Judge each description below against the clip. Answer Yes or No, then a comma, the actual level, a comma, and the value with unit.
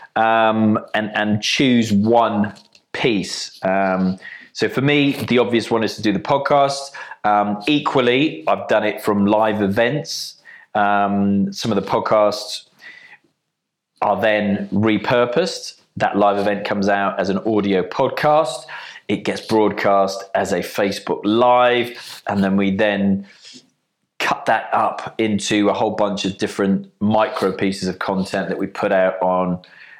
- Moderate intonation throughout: No, narrow, 2.2 semitones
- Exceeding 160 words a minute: No, average, 145 wpm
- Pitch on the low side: Yes, low, 105 Hz